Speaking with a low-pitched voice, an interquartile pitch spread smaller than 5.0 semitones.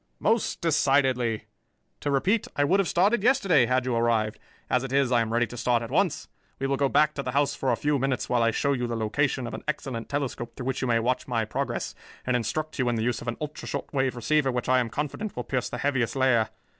Yes: low, 130 Hz; average, 3.3 semitones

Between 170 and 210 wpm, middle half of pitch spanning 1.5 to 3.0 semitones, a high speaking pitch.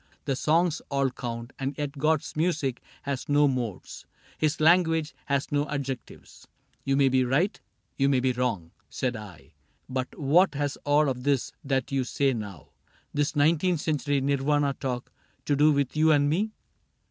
No: average, 175 wpm; narrow, 2.5 semitones; medium, 140 Hz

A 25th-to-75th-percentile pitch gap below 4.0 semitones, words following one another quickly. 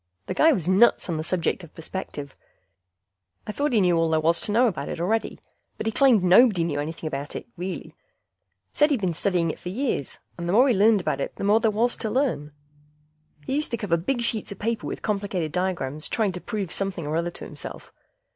No: average, 5.1 semitones; fast, 225 wpm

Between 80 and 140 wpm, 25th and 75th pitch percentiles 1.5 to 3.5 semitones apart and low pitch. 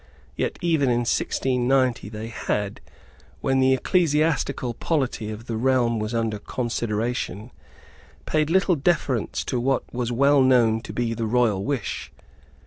Yes: slow, 135 wpm; average, 3.1 semitones; low, 125 Hz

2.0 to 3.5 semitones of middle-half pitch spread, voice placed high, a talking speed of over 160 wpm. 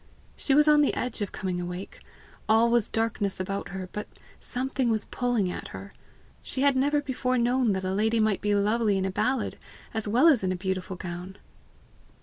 No: average, 4.8 semitones; high, 215 Hz; average, 195 wpm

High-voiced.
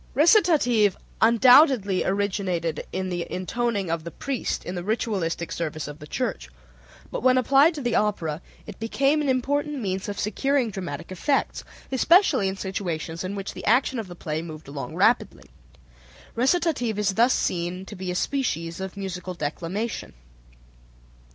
Yes: high, 200 Hz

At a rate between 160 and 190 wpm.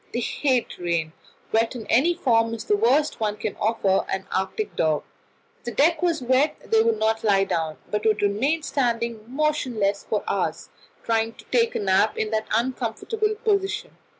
Yes: average, 180 wpm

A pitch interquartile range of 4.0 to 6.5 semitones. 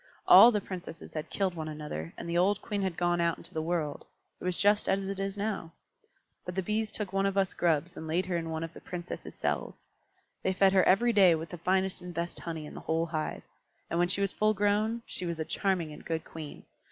No: average, 3.1 semitones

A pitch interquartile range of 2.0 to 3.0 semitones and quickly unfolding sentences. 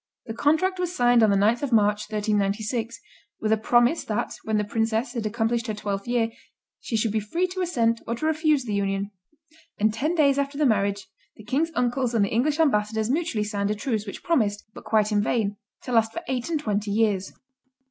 No: average, 4.0 semitones; fast, 210 wpm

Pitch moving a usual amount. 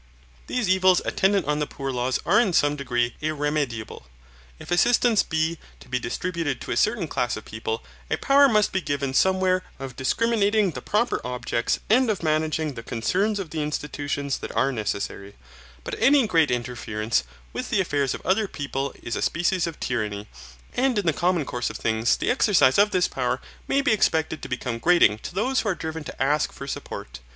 No: wide, 7.3 semitones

